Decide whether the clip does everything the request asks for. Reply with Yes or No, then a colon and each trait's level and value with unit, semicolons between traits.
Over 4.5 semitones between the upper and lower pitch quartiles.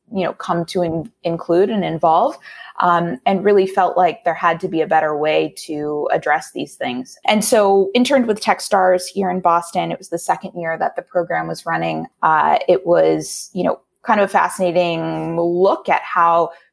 No: average, 2.9 semitones